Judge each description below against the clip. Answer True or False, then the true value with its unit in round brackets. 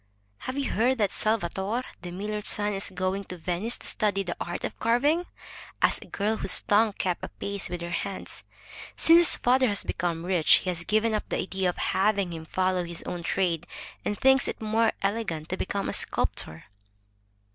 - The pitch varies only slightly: False (3.7 semitones)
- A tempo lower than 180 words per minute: False (190 wpm)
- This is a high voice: True (195 Hz)